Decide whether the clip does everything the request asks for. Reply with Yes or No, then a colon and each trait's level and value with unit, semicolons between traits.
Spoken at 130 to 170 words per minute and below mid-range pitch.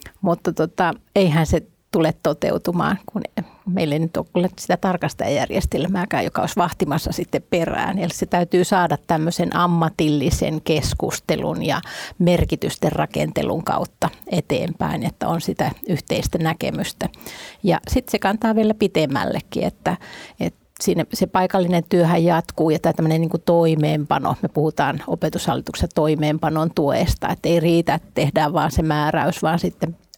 No: average, 135 wpm; medium, 170 Hz